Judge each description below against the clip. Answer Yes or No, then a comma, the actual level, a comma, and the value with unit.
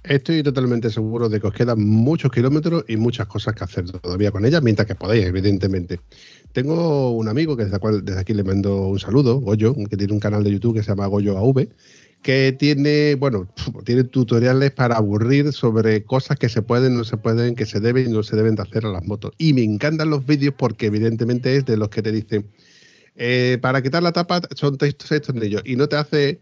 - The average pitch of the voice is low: Yes, low, 120 Hz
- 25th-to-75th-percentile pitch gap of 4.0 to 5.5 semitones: Yes, average, 4.6 semitones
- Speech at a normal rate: No, fast, 225 wpm